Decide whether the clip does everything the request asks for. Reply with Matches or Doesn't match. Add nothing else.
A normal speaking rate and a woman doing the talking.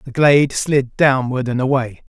Doesn't match